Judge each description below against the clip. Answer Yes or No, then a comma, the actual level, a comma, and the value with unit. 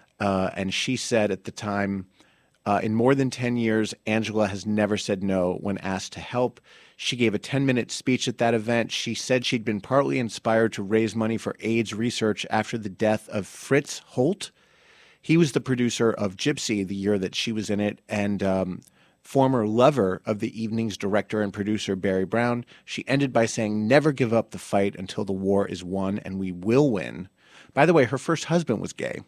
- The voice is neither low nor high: No, low, 110 Hz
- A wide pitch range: No, average, 3.2 semitones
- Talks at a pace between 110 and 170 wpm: No, fast, 205 wpm